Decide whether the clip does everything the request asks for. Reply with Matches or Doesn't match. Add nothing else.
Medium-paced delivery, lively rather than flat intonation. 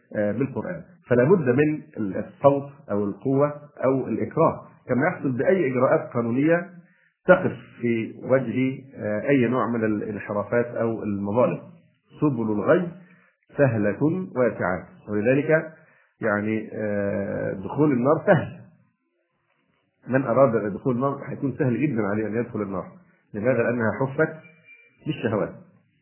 Matches